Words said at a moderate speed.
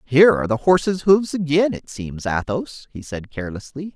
Yes: average, 180 wpm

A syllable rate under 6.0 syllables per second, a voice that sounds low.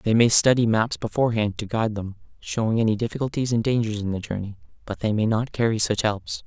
No: 6.1 syllables/s; low, 110 Hz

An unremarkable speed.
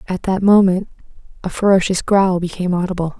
Yes: average, 150 wpm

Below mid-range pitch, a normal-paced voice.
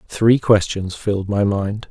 Yes: low, 105 Hz; average, 155 wpm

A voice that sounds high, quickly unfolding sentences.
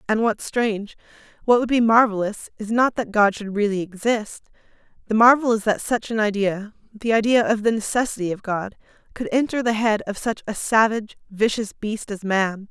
No: high, 215 Hz; average, 190 wpm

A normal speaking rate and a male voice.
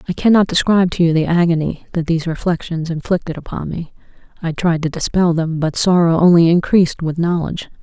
No: average, 185 wpm; female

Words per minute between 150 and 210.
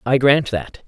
Yes: fast, 205 wpm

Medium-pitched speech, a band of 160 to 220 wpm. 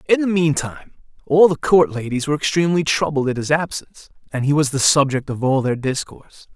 Yes: medium, 150 Hz; average, 200 wpm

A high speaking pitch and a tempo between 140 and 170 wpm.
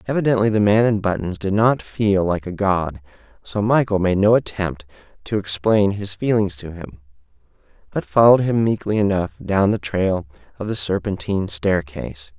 No: very low, 95 Hz; average, 165 wpm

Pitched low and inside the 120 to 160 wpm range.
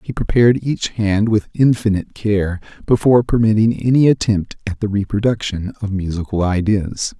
Yes: low, 105 Hz; average, 140 wpm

